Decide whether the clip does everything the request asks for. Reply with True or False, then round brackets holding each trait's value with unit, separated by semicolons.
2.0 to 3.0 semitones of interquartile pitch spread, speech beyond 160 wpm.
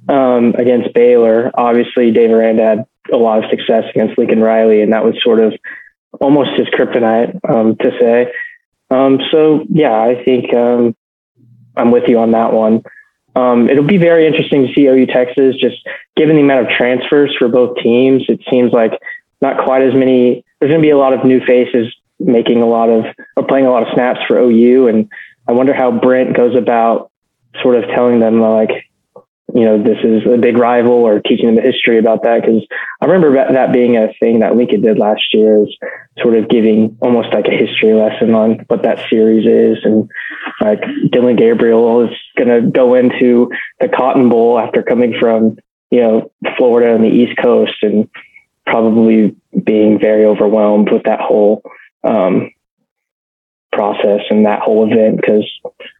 True (2.4 semitones; 180 wpm)